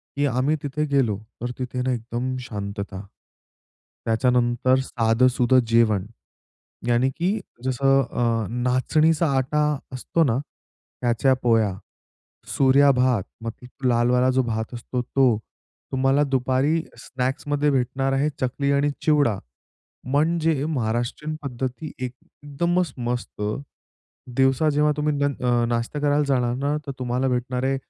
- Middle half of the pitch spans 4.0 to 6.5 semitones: No, average, 2.9 semitones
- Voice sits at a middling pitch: No, low, 130 Hz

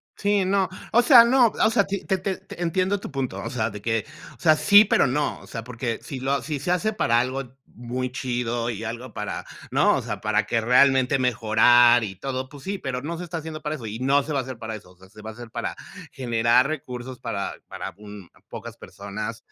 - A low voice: Yes, low, 125 Hz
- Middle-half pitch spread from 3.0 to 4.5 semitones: No, average, 5.2 semitones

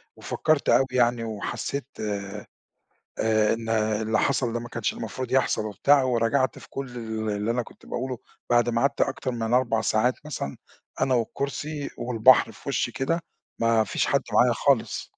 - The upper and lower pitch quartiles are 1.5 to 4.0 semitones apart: Yes, average, 2.8 semitones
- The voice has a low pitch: Yes, low, 120 Hz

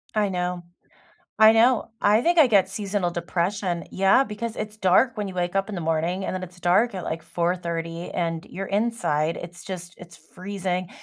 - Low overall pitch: No, medium, 185 Hz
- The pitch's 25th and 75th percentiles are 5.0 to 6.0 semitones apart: No, average, 3.1 semitones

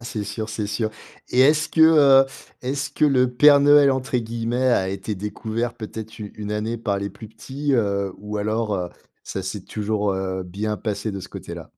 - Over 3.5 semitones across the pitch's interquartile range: Yes, average, 3.9 semitones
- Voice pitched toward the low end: Yes, low, 110 Hz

